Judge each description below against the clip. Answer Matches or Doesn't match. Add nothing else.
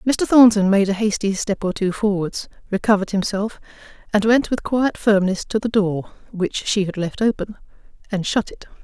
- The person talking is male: Doesn't match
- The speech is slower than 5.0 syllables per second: Matches